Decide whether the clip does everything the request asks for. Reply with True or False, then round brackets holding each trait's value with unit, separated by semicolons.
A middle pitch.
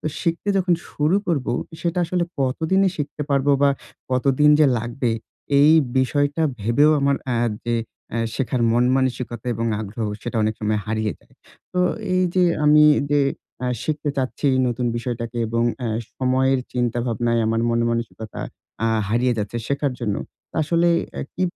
False (130 Hz)